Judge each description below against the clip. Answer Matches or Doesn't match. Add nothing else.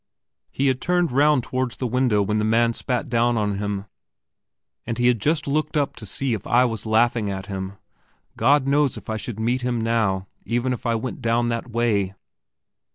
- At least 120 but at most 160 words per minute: Doesn't match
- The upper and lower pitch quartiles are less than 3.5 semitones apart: Matches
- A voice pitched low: Matches